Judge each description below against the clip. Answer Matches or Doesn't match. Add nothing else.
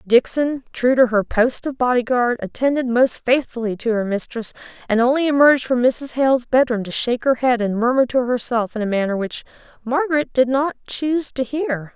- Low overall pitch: Doesn't match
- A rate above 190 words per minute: Matches